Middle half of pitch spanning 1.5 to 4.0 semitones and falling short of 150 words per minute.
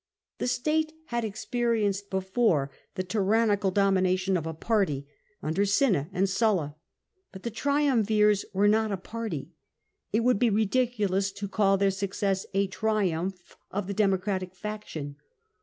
Yes: average, 2.7 semitones; average, 140 wpm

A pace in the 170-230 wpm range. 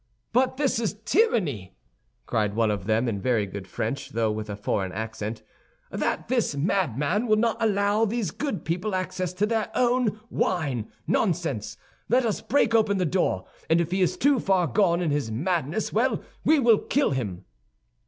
Yes: average, 175 wpm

